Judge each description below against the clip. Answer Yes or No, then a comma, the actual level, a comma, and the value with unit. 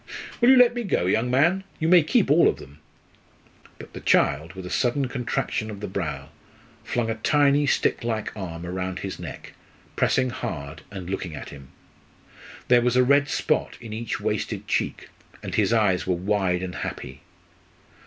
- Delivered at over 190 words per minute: No, average, 180 wpm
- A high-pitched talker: No, low, 110 Hz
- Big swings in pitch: Yes, wide, 7.1 semitones